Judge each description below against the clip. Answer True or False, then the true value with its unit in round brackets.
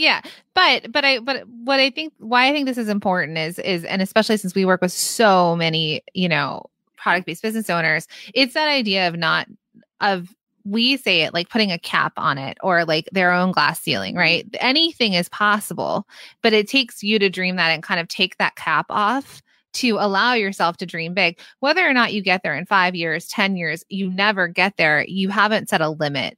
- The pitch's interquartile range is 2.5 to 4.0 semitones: False (4.7 semitones)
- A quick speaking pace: True (215 wpm)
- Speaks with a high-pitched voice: True (195 Hz)